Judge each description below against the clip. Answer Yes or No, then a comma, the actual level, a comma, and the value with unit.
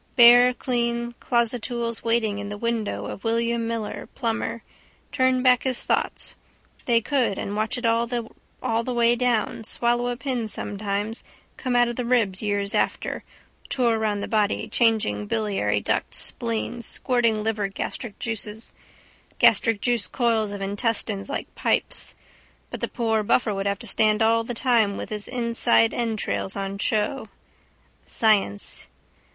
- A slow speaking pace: No, average, 145 wpm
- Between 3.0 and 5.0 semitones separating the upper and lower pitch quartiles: No, narrow, 2.6 semitones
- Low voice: No, high, 225 Hz